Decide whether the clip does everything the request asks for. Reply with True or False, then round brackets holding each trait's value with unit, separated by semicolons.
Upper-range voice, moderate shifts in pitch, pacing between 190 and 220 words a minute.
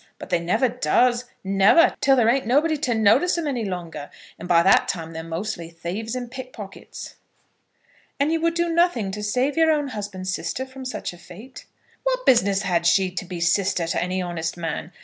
False (210 Hz; 6.8 semitones; 195 wpm)